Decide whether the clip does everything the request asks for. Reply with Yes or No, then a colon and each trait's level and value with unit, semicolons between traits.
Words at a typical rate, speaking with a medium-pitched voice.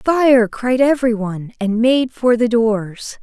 No: average, 165 wpm; high, 235 Hz